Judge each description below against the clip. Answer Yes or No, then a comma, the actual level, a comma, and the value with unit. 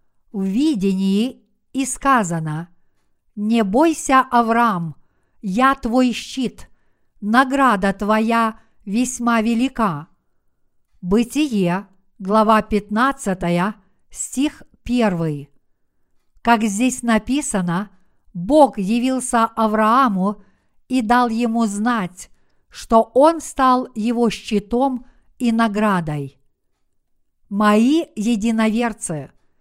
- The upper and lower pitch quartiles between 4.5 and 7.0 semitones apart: No, average, 4.0 semitones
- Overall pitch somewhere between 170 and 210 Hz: No, high, 225 Hz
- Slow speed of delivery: Yes, slow, 75 wpm